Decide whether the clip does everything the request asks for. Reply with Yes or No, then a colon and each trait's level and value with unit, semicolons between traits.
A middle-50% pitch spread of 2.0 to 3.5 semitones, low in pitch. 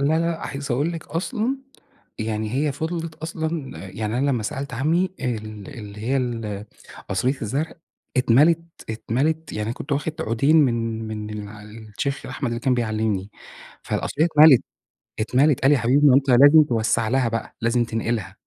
No: average, 5.0 semitones; low, 125 Hz